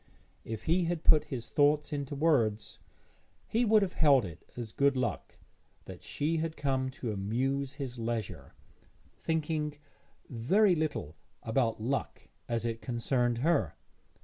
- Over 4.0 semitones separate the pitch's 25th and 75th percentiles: Yes, average, 4.9 semitones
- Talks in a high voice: No, low, 135 Hz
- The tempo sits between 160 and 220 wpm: No, average, 140 wpm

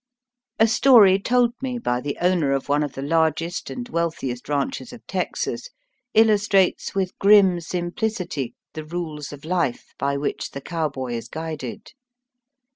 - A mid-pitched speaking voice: Yes, medium, 170 Hz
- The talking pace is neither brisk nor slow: Yes, average, 145 wpm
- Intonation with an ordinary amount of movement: No, wide, 5.7 semitones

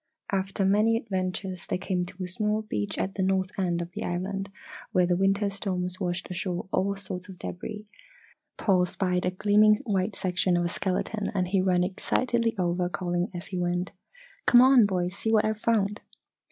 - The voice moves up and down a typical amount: No, narrow, 2.3 semitones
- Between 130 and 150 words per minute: No, average, 185 wpm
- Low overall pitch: No, high, 190 Hz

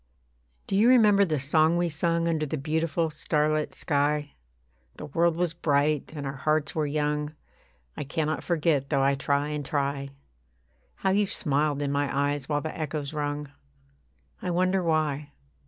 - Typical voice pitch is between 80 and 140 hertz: No, medium, 150 Hz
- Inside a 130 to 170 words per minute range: Yes, average, 160 wpm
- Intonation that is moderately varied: No, narrow, 2.3 semitones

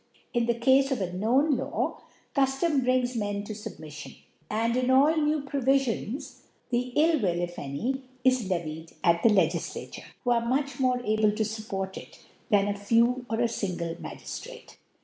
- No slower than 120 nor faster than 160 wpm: No, average, 170 wpm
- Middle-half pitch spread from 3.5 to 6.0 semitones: Yes, average, 4.7 semitones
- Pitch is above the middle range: Yes, high, 235 Hz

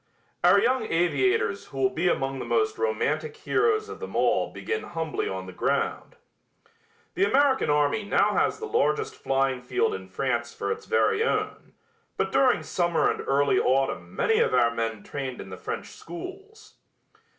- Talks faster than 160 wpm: Yes, average, 170 wpm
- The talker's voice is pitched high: No, medium, 180 Hz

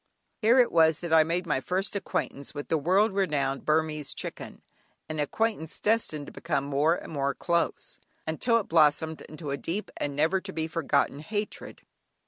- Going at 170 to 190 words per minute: Yes, average, 175 wpm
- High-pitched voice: No, medium, 160 Hz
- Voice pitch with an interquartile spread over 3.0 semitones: Yes, average, 4.3 semitones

